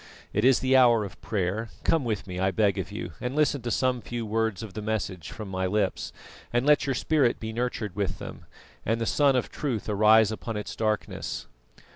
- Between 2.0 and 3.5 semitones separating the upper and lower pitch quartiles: Yes, average, 3.0 semitones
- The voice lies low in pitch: Yes, low, 110 Hz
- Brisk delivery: Yes, fast, 210 wpm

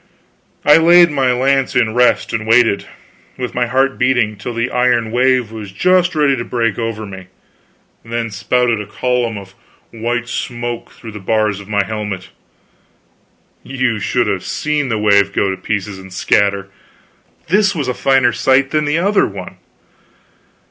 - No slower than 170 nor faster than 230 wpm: No, average, 160 wpm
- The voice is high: No, low, 120 Hz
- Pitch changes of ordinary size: Yes, average, 3.8 semitones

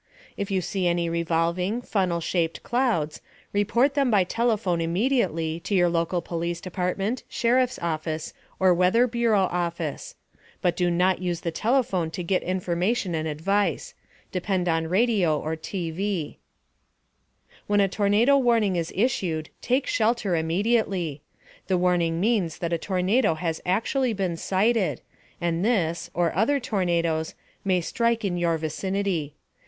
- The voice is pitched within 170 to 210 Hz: Yes, medium, 185 Hz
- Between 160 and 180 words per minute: No, average, 140 wpm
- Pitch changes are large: No, average, 4.2 semitones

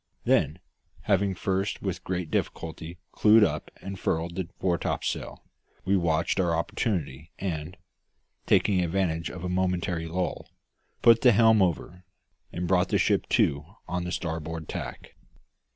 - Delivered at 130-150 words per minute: Yes, average, 140 wpm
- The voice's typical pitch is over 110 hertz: No, very low, 90 Hz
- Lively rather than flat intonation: No, average, 2.7 semitones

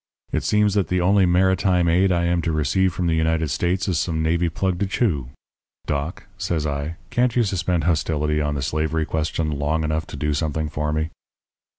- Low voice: Yes, very low, 80 Hz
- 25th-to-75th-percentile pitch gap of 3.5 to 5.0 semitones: No, average, 3.1 semitones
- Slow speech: No, average, 200 wpm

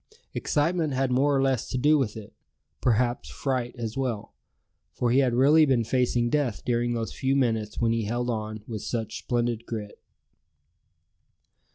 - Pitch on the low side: Yes, low, 120 Hz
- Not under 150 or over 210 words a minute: Yes, average, 165 wpm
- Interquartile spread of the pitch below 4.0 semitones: Yes, average, 2.8 semitones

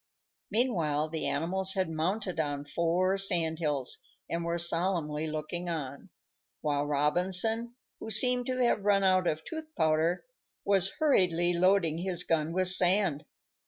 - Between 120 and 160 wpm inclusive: Yes, average, 140 wpm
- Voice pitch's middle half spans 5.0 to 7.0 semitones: No, average, 3.6 semitones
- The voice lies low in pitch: No, medium, 175 Hz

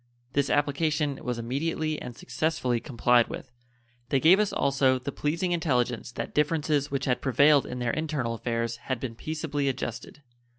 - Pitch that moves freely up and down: No, average, 3.7 semitones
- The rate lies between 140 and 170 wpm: Yes, average, 160 wpm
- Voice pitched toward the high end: No, medium, 140 Hz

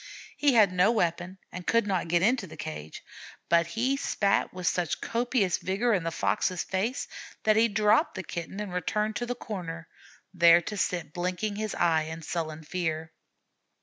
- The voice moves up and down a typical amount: Yes, average, 4.2 semitones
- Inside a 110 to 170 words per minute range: No, average, 180 wpm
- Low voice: No, medium, 185 Hz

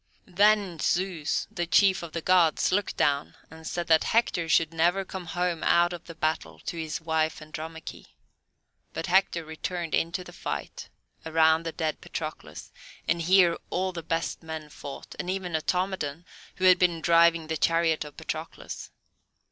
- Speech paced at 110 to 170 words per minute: Yes, average, 165 wpm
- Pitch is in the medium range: Yes, medium, 165 Hz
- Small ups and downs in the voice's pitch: Yes, narrow, 2.1 semitones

